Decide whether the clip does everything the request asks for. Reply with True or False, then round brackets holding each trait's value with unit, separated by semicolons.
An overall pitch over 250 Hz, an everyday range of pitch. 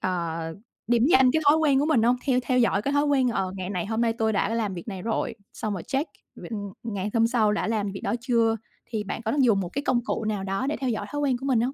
False (225 Hz; 4.1 semitones)